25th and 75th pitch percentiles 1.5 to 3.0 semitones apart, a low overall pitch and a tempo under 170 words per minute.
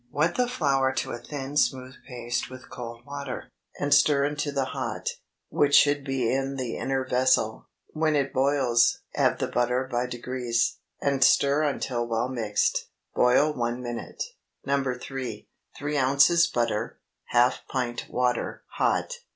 Yes: average, 2.7 semitones; low, 130 Hz; average, 150 wpm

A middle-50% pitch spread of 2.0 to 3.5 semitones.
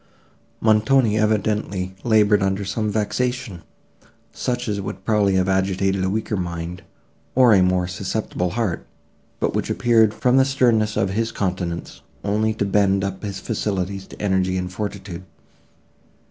Yes: narrow, 2.6 semitones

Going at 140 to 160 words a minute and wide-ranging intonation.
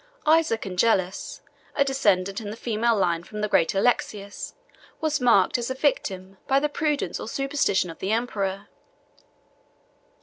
Yes: average, 145 wpm; wide, 5.7 semitones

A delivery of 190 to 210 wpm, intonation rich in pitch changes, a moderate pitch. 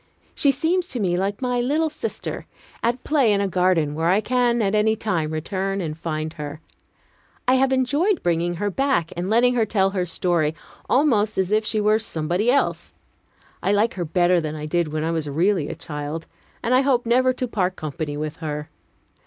No: average, 200 wpm; wide, 6.8 semitones; high, 195 Hz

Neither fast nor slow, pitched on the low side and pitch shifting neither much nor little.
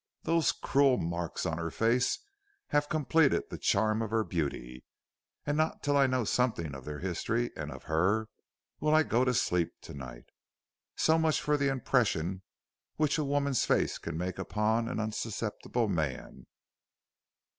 No: average, 160 wpm; low, 115 Hz; wide, 8.6 semitones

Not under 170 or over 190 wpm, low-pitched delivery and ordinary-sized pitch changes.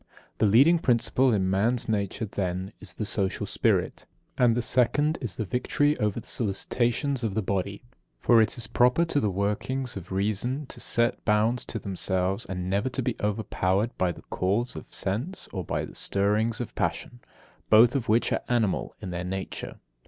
Yes: average, 180 wpm; low, 110 Hz; average, 4.0 semitones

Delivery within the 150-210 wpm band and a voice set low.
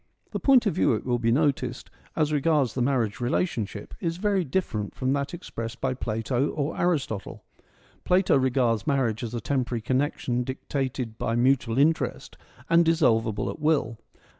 Yes: average, 160 wpm; low, 130 Hz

